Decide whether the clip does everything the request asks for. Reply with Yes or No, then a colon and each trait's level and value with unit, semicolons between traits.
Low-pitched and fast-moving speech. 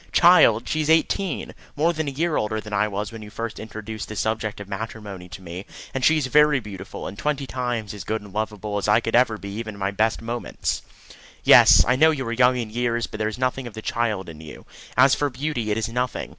Yes: low, 110 Hz; fast, 245 wpm